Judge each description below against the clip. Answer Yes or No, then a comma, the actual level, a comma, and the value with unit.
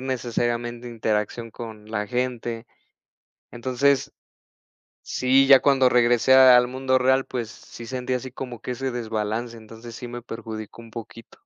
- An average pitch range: No, narrow, 2.0 semitones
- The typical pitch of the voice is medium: No, low, 120 Hz